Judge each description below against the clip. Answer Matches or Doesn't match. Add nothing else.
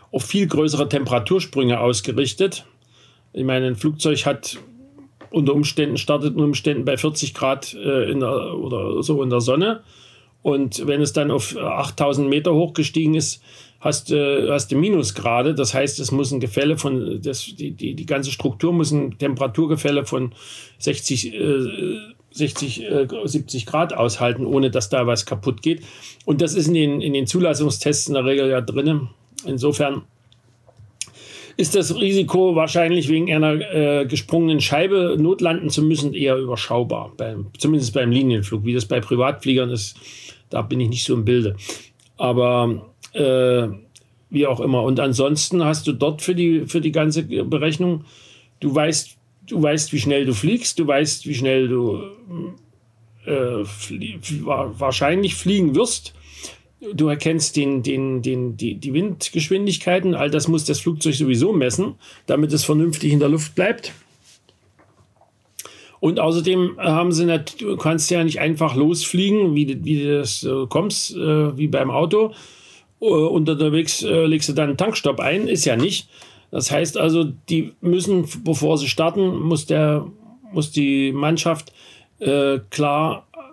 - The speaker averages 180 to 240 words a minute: Doesn't match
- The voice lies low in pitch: Doesn't match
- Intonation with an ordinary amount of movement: Matches